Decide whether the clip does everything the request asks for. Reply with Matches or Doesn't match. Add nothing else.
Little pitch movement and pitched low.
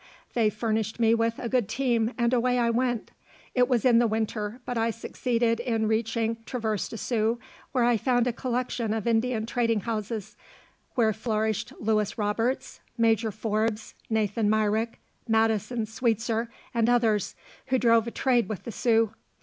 Doesn't match